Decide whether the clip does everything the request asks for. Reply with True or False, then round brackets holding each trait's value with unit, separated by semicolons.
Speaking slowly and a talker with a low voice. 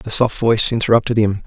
False (205 wpm; 110 Hz)